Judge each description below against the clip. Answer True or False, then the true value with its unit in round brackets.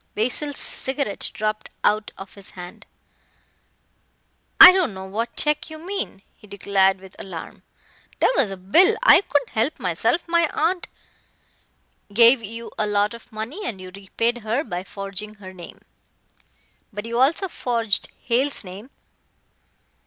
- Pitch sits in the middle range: False (220 Hz)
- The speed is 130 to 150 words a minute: True (145 wpm)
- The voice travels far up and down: True (6.2 semitones)